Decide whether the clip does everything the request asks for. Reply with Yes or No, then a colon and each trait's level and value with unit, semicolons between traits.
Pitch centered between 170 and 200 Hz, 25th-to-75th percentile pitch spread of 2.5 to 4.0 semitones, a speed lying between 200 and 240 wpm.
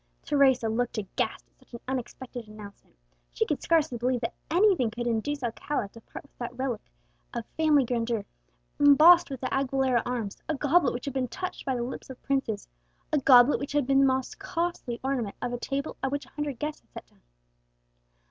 No: very high, 260 Hz; average, 3.1 semitones; fast, 205 wpm